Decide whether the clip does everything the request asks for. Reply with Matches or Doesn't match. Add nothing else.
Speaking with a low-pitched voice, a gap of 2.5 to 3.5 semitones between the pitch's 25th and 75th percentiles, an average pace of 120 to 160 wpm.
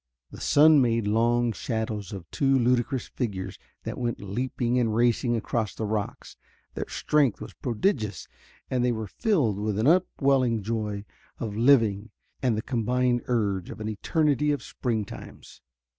Matches